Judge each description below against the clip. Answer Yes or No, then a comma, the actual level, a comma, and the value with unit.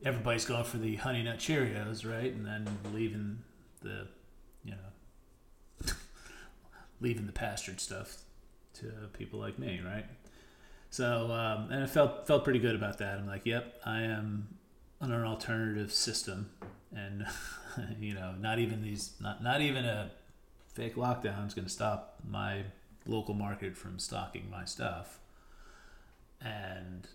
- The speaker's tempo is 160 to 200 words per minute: No, average, 145 wpm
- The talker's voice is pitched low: Yes, low, 110 Hz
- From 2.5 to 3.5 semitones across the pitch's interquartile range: Yes, average, 2.8 semitones